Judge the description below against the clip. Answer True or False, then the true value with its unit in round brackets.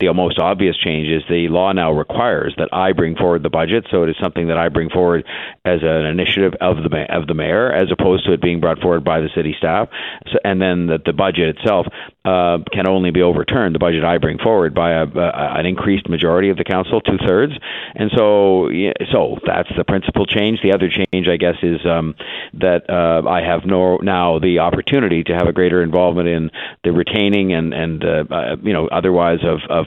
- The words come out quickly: True (220 wpm)